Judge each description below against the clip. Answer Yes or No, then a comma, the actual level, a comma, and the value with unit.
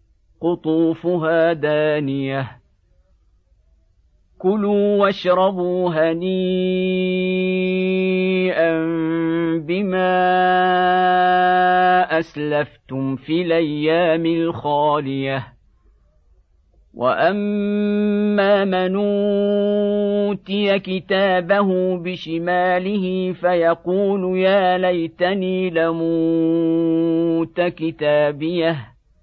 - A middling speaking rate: No, slow, 40 wpm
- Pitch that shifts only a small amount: No, average, 3.5 semitones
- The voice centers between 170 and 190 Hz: Yes, medium, 175 Hz